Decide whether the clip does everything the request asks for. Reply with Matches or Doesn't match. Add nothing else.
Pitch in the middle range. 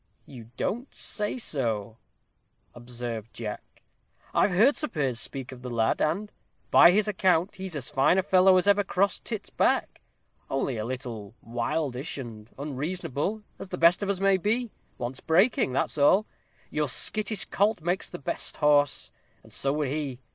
Matches